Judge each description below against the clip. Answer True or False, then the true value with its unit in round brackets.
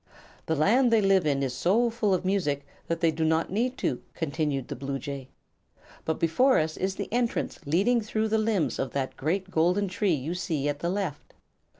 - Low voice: False (170 Hz)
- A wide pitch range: True (5.8 semitones)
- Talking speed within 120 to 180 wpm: False (200 wpm)